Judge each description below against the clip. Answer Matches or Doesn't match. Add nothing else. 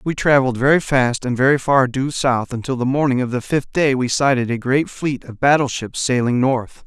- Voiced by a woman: Doesn't match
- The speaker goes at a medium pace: Doesn't match